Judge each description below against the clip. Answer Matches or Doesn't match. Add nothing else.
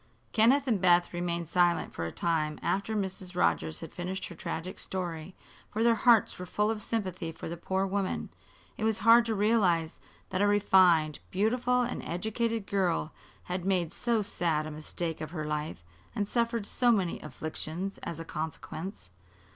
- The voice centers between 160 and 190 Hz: Matches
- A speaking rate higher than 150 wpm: Matches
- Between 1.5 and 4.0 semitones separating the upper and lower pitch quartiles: Doesn't match